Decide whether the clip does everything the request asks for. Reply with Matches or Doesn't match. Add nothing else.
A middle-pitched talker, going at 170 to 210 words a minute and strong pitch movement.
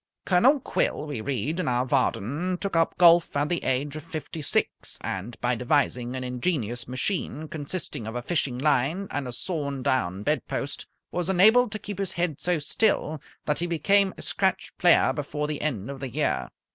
Matches